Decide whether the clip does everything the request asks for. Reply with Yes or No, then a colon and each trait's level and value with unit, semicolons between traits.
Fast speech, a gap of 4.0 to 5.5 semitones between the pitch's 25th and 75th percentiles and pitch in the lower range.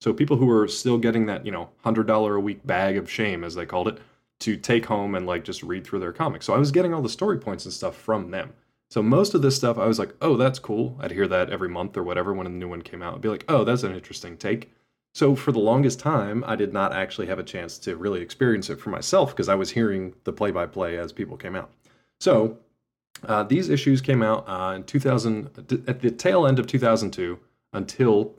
Yes: fast, 250 wpm; average, 4.3 semitones; low, 110 Hz